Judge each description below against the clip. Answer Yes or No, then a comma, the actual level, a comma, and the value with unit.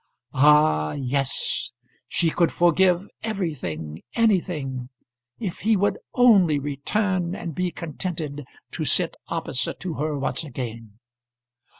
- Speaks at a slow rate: Yes, slow, 110 wpm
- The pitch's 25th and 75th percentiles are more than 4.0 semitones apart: Yes, average, 5.2 semitones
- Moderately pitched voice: Yes, medium, 155 Hz